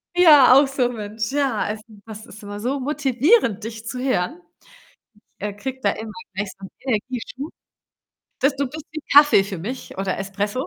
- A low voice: No, high, 245 Hz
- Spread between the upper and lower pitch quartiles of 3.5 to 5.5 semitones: Yes, average, 5.0 semitones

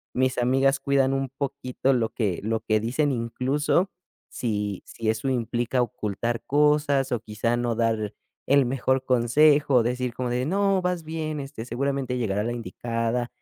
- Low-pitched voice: Yes, low, 125 Hz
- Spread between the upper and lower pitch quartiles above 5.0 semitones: No, average, 3.2 semitones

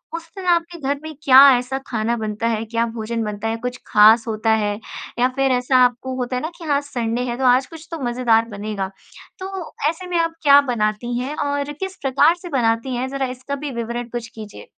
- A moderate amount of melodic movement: Yes, average, 3.9 semitones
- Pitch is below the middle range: No, very high, 250 Hz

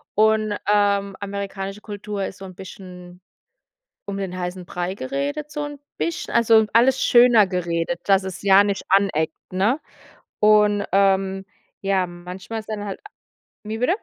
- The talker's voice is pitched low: No, high, 200 Hz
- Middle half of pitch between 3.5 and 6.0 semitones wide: No, narrow, 2.4 semitones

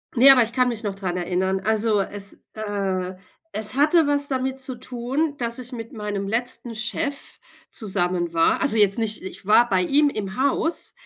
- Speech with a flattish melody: No, average, 4.8 semitones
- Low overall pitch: No, high, 220 Hz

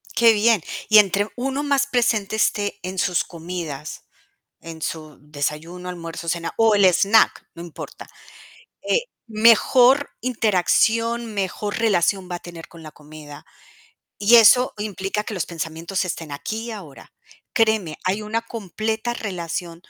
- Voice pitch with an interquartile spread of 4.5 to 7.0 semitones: Yes, average, 5.0 semitones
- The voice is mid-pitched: No, high, 195 Hz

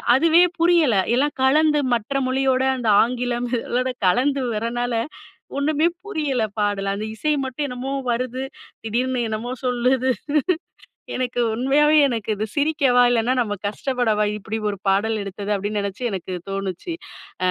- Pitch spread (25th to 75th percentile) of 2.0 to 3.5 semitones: No, average, 4.0 semitones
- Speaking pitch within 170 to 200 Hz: No, high, 245 Hz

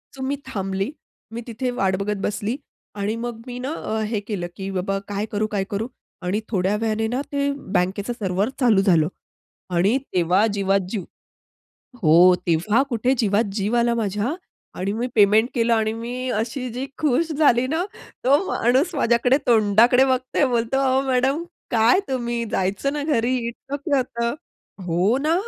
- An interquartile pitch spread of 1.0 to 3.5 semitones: No, average, 4.0 semitones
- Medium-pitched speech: No, high, 230 Hz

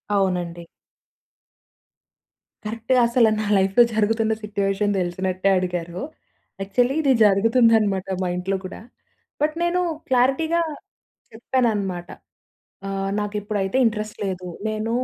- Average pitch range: Yes, average, 3.1 semitones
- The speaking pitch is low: No, high, 210 Hz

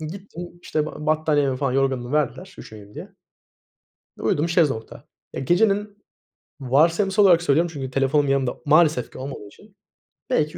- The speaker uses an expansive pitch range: No, average, 4.4 semitones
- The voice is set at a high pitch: No, medium, 155 Hz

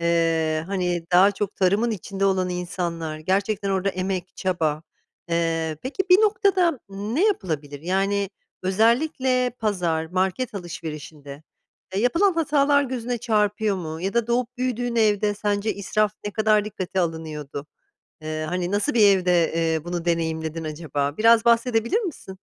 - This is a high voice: Yes, high, 195 Hz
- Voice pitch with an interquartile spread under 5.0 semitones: No, wide, 5.4 semitones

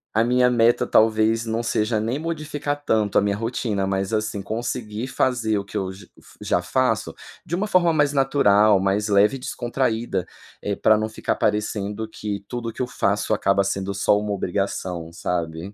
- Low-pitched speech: Yes, low, 110 Hz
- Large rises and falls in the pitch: No, average, 3.3 semitones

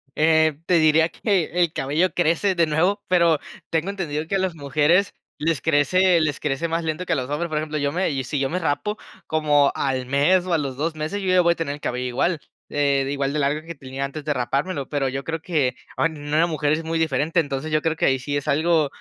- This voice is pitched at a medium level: Yes, medium, 155 Hz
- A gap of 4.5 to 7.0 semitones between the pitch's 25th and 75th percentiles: No, average, 2.9 semitones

